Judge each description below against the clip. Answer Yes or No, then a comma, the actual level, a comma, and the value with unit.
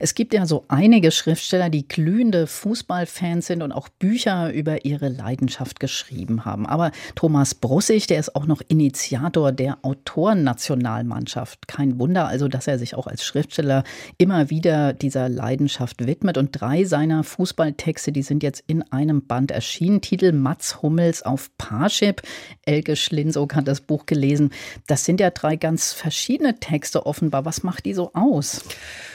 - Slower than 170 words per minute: Yes, average, 160 wpm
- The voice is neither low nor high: Yes, medium, 150 Hz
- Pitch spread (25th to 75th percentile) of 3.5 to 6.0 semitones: Yes, average, 3.9 semitones